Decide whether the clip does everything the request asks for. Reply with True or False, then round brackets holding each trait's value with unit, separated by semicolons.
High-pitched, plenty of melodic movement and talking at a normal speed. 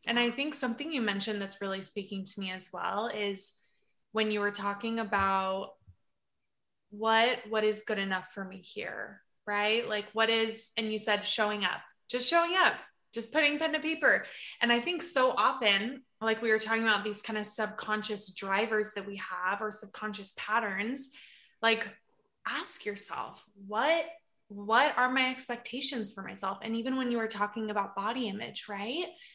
False (215 Hz; 3.0 semitones; 175 wpm)